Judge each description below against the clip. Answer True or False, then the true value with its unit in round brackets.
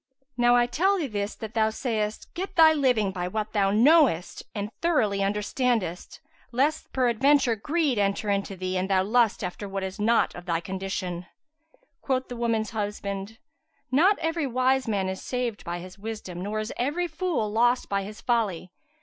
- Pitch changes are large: False (4.5 semitones)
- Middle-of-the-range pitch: False (220 Hz)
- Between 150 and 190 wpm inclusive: True (175 wpm)